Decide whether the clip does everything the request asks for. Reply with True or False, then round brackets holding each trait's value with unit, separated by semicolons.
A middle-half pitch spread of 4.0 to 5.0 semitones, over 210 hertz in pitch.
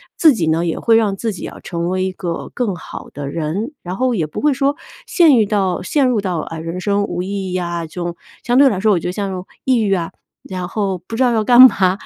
False (4.7 semitones; 195 Hz)